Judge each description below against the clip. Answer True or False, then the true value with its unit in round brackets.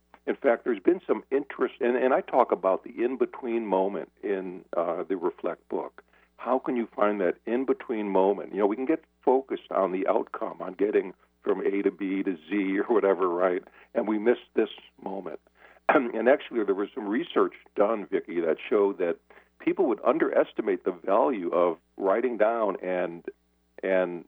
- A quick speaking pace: False (185 wpm)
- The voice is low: False (160 Hz)